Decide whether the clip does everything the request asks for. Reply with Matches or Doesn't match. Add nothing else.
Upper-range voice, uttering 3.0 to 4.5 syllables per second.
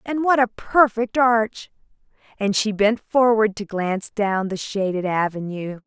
Matches